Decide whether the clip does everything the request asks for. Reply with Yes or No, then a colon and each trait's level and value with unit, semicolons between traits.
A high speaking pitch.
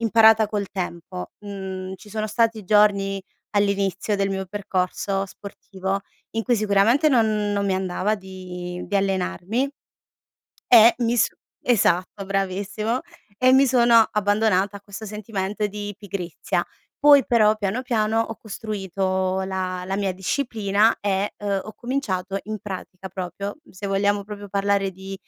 Yes: high, 200 Hz